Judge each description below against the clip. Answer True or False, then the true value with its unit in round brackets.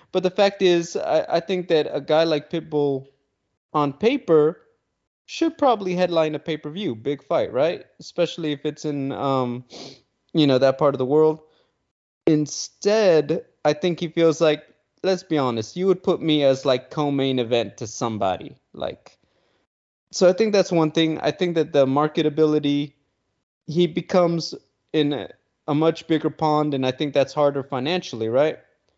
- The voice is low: False (155 Hz)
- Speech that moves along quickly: False (165 wpm)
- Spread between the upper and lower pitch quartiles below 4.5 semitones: True (3.6 semitones)